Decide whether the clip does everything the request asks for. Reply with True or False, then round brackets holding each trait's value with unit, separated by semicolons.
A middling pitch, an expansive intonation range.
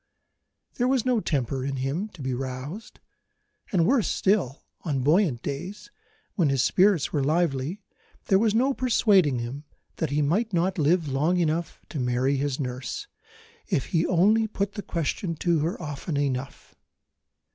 True (160 Hz; 6.2 semitones)